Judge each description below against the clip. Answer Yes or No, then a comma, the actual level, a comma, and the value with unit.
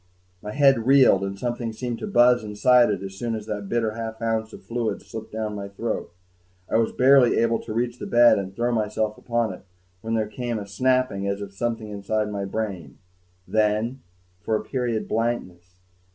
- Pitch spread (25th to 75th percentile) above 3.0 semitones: No, narrow, 2.5 semitones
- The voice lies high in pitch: No, low, 110 Hz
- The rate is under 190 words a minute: No, average, 195 wpm